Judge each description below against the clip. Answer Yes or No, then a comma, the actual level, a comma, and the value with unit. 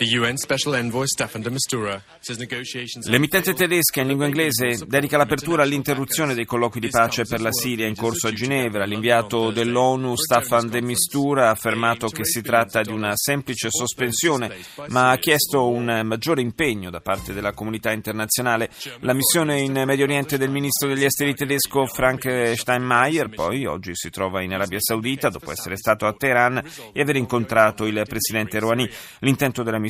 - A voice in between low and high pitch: No, low, 120 Hz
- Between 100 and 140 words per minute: No, average, 155 wpm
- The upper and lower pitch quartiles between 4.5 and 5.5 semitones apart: No, average, 3.6 semitones